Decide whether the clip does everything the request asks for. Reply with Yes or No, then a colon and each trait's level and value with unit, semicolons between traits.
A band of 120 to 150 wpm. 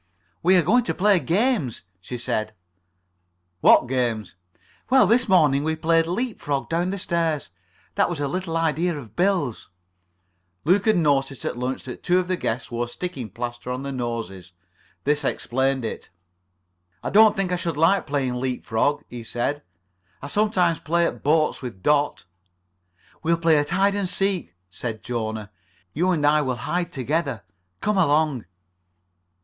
No: average, 165 wpm